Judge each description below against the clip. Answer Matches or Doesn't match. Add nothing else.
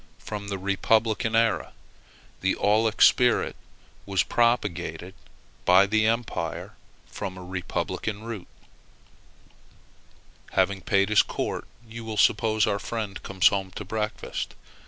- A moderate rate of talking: Doesn't match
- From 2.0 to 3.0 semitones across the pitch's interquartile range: Matches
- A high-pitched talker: Doesn't match